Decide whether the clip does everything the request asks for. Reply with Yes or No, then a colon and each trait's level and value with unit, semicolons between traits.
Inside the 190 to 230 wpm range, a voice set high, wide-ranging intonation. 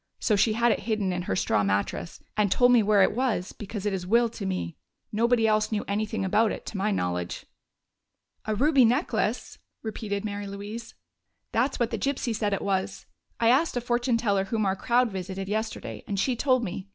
No: average, 200 wpm; high, 215 Hz; average, 3.3 semitones